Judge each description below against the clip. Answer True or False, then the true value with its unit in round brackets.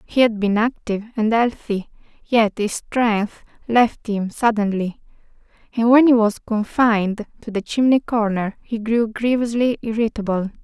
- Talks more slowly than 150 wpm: True (140 wpm)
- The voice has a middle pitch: False (220 Hz)